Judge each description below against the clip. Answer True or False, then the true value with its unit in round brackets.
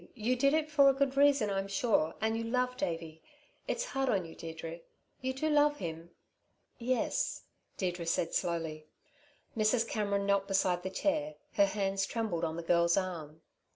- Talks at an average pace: True (170 wpm)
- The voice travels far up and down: True (6.9 semitones)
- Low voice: False (200 Hz)